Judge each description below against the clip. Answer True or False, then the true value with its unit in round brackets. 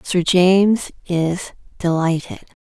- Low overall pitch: False (180 Hz)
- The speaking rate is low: True (90 wpm)